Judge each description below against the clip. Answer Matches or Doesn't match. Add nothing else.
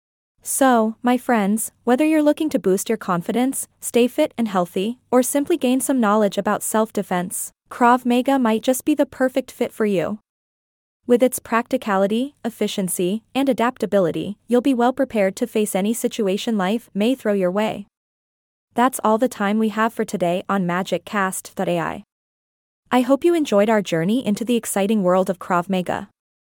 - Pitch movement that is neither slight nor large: Matches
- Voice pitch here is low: Doesn't match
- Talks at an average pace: Matches